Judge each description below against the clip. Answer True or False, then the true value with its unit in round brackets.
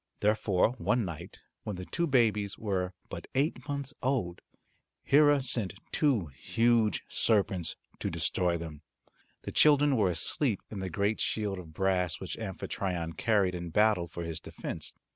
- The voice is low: True (100 Hz)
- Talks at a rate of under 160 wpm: True (150 wpm)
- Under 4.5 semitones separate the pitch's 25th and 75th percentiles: False (5.1 semitones)